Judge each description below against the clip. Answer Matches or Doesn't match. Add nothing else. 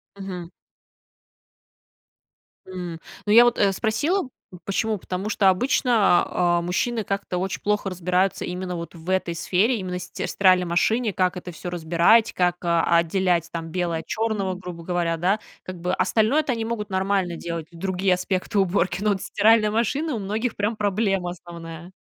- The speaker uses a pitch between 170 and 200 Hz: Matches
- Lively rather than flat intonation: Doesn't match